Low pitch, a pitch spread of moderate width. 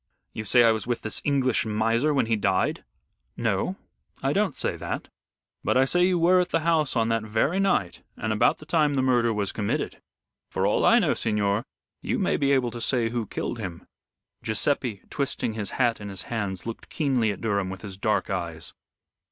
Yes: low, 115 Hz; average, 4.6 semitones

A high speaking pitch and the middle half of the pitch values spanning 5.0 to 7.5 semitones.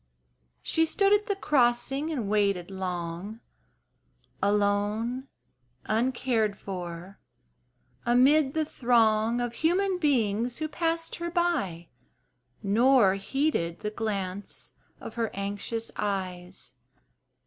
Yes: high, 225 Hz; wide, 5.6 semitones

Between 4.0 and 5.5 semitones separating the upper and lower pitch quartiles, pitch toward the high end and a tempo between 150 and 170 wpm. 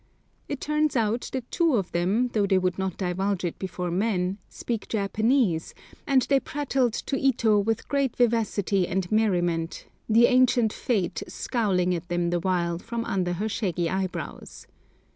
Yes: average, 4.9 semitones; high, 205 Hz; average, 160 wpm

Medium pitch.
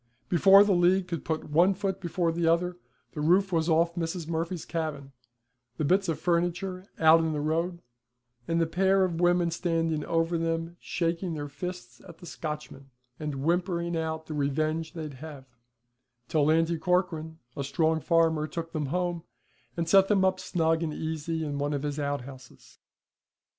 Yes: medium, 165 Hz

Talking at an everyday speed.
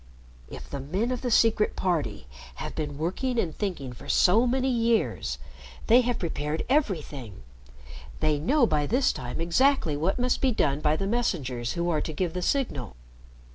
Yes: average, 175 wpm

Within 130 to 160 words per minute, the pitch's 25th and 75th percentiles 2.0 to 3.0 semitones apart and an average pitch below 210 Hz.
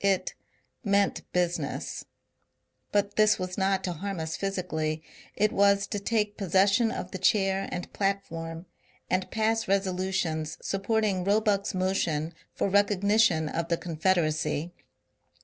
Yes: slow, 135 wpm; average, 2.7 semitones; high, 190 Hz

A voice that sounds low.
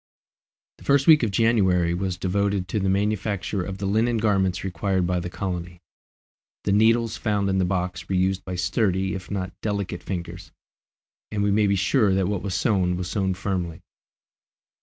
Yes: very low, 95 Hz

